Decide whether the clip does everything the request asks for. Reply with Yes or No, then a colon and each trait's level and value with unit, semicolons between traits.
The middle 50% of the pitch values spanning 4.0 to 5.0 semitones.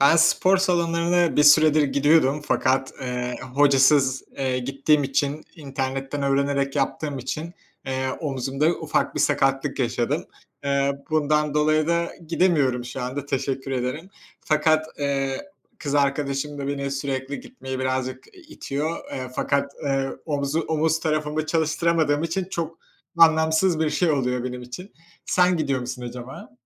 No: average, 2.8 semitones